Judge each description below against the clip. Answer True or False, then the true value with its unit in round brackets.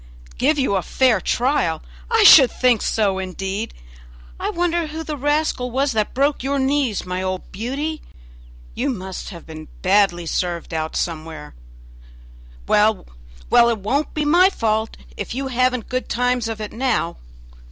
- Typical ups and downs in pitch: False (6.6 semitones)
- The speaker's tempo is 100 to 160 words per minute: True (155 wpm)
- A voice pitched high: True (235 Hz)